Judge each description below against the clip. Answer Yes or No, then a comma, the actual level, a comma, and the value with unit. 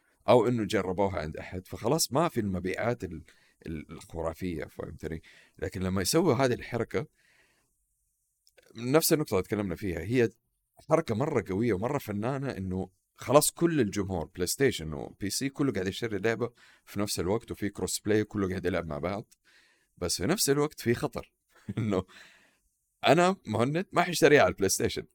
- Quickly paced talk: Yes, fast, 155 wpm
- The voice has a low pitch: Yes, low, 100 Hz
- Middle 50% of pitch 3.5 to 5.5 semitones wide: Yes, average, 5.2 semitones